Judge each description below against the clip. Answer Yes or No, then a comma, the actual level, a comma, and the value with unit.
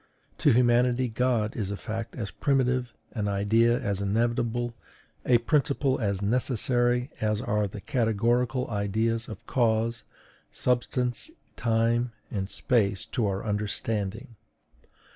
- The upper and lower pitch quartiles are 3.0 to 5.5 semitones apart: No, narrow, 2.6 semitones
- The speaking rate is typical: No, slow, 120 wpm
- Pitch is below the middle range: Yes, low, 115 Hz